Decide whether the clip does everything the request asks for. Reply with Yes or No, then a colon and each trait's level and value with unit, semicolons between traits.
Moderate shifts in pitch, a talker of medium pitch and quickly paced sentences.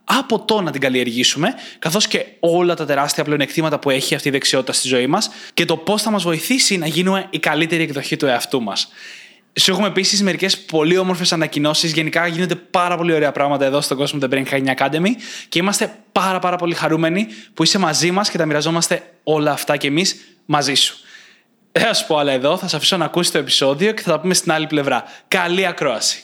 Yes: average, 4.0 semitones; medium, 165 Hz; fast, 215 wpm